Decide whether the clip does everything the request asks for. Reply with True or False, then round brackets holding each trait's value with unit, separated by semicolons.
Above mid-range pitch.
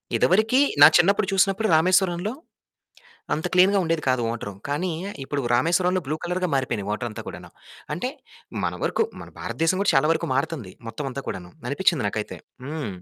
False (165 Hz)